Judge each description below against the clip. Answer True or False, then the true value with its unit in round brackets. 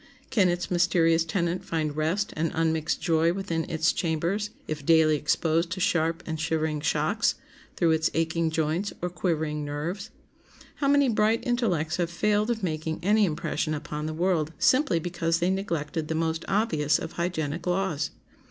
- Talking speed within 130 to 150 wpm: False (160 wpm)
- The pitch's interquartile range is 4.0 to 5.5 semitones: False (2.6 semitones)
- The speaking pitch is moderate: True (165 Hz)